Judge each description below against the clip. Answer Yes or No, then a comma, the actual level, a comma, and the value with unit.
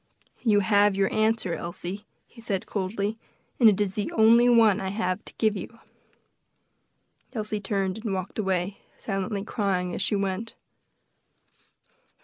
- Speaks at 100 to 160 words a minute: Yes, average, 140 wpm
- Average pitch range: No, narrow, 2.3 semitones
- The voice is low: No, high, 205 Hz